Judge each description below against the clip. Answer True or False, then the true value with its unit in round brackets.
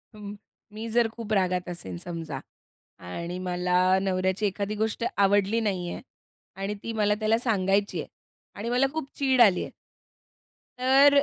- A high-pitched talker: True (205 Hz)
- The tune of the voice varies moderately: True (3.5 semitones)